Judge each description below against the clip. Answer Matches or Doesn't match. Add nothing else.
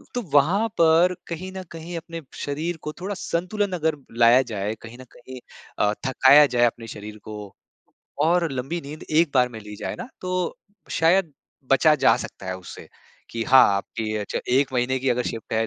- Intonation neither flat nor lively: Doesn't match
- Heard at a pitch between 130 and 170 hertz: Matches